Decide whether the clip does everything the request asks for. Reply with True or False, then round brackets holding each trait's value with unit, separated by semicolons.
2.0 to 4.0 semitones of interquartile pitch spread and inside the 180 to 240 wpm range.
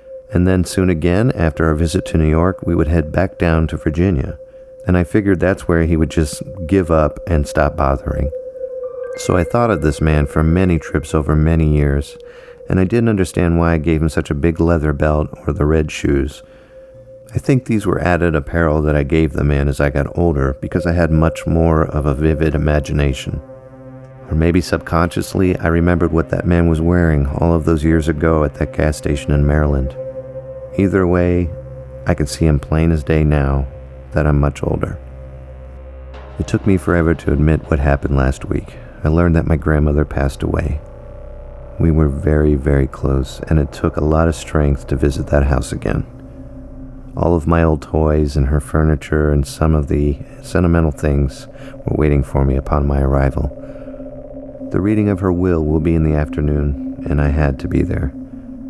True (3.6 semitones; 195 wpm)